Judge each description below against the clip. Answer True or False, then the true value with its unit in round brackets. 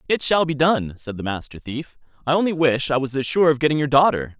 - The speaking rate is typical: False (260 wpm)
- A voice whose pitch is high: False (145 Hz)